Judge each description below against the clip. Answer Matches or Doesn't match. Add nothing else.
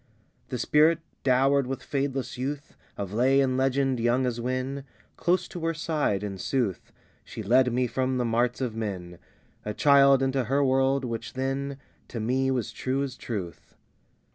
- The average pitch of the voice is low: Matches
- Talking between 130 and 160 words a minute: Doesn't match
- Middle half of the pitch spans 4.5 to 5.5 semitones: Doesn't match